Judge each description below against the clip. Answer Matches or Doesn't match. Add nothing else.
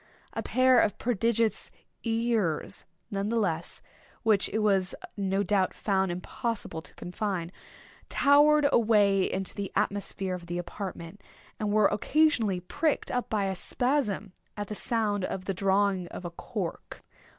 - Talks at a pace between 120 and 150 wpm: Matches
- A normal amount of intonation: Matches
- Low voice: Doesn't match